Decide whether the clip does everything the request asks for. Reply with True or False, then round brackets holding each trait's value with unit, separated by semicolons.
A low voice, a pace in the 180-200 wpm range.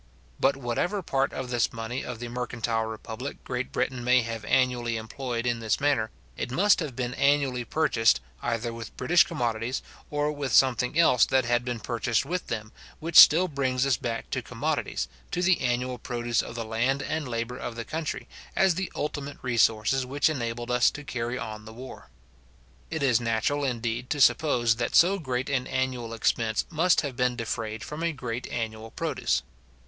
True (125 Hz; 185 wpm)